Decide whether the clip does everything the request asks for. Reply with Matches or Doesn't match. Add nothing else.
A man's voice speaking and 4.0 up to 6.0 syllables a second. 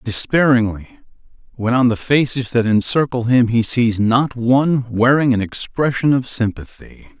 Matches